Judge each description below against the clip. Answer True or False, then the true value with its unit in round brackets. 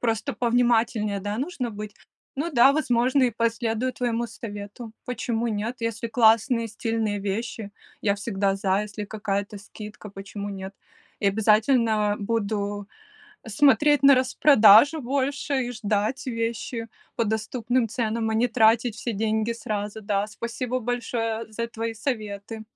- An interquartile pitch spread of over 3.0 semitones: False (2.5 semitones)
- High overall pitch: True (225 Hz)